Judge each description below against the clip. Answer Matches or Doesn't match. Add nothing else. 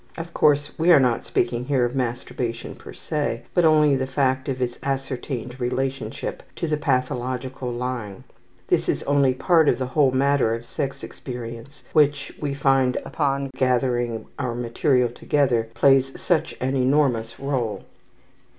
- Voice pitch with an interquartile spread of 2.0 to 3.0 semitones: Matches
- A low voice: Matches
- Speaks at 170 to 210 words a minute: Doesn't match